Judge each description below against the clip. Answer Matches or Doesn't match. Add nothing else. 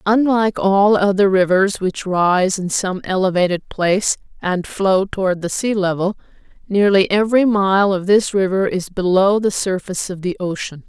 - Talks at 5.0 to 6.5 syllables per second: Doesn't match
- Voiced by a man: Doesn't match